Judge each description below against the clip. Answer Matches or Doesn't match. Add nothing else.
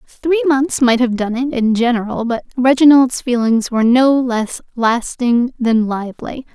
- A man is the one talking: Doesn't match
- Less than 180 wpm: Matches